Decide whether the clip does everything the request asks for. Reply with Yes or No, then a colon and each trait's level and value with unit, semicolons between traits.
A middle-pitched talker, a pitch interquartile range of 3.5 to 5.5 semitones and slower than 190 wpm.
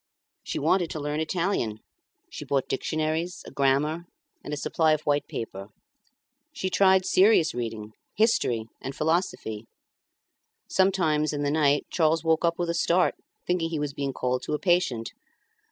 Yes: medium, 155 Hz; average, 3.9 semitones; average, 155 wpm